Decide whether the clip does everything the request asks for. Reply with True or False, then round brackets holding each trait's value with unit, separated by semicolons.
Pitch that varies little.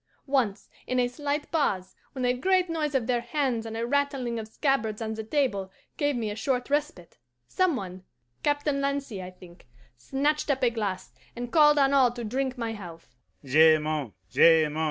False (4.5 semitones)